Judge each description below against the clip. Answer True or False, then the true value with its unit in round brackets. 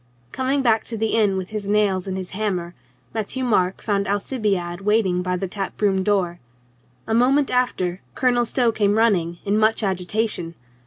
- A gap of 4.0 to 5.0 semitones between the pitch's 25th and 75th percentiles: False (3.2 semitones)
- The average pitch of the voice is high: True (205 Hz)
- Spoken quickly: False (170 wpm)